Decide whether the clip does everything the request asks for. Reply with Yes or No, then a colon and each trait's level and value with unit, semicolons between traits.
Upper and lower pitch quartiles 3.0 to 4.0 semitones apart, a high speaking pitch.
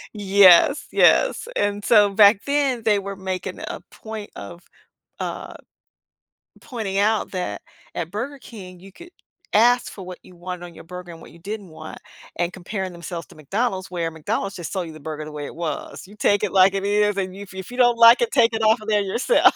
Yes: average, 3.5 semitones; high, 195 Hz